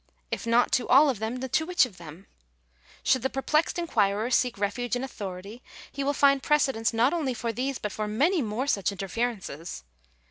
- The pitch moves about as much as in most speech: Yes, average, 4.5 semitones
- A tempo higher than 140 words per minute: Yes, average, 185 wpm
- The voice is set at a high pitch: Yes, high, 245 Hz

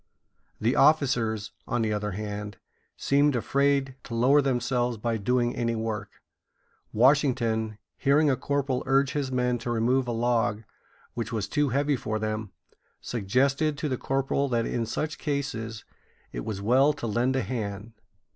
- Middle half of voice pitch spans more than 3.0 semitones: Yes, average, 3.6 semitones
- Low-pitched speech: Yes, low, 120 Hz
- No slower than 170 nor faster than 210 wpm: No, average, 155 wpm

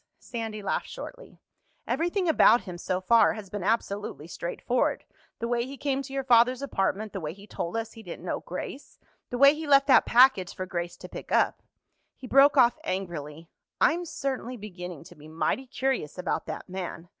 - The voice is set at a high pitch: Yes, high, 225 Hz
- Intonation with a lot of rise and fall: Yes, wide, 6.7 semitones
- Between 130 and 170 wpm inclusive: No, average, 185 wpm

